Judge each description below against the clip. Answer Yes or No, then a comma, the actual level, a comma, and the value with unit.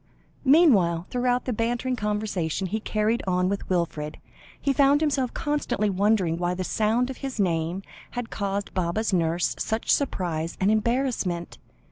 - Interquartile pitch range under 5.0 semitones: No, wide, 5.5 semitones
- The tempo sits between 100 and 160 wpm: Yes, average, 145 wpm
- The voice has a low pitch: No, high, 210 Hz